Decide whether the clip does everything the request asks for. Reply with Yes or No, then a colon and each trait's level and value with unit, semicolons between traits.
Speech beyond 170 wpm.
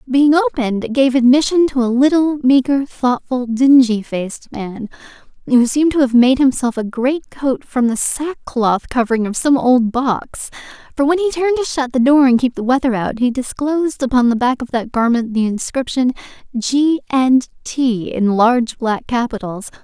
Yes: average, 180 wpm